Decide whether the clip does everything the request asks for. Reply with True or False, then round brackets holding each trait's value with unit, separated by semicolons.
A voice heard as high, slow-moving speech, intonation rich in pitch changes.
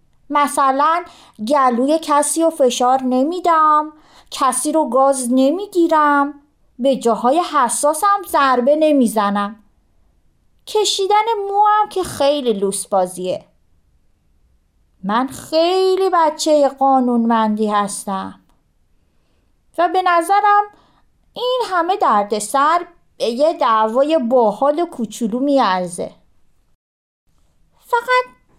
True (275 Hz; 85 wpm; 7.2 semitones)